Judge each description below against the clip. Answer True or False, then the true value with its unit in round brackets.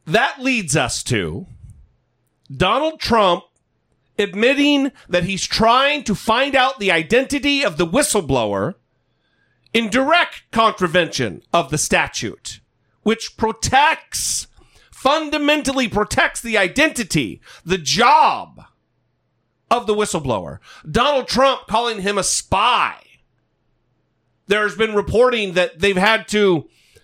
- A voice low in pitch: False (220 Hz)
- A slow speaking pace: True (105 wpm)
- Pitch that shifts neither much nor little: False (6.4 semitones)